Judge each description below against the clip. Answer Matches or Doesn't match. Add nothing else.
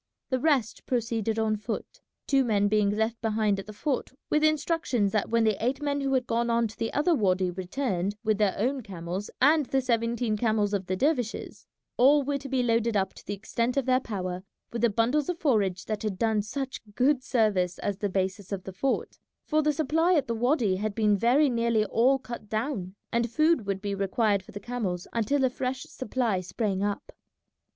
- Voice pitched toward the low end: Doesn't match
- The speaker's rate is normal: Doesn't match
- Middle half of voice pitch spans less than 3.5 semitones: Doesn't match